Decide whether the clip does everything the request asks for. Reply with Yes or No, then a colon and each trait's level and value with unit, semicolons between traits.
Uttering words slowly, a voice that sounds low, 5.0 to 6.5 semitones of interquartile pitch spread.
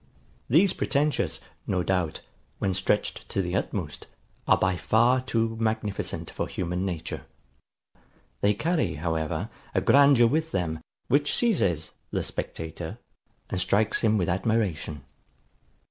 Yes: slow, 125 wpm; low, 100 Hz; wide, 5.6 semitones